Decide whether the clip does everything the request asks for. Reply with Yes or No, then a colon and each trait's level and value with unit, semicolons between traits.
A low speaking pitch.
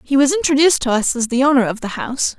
No: very high, 265 Hz